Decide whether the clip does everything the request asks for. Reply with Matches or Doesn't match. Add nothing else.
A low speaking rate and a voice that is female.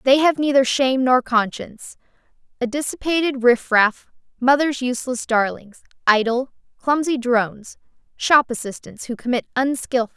Matches